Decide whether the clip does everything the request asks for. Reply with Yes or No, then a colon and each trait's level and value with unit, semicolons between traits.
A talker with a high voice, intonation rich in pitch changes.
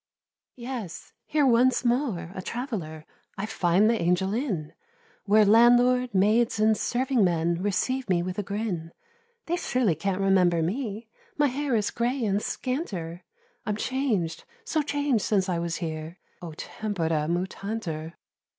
Yes: high, 205 Hz; wide, 5.8 semitones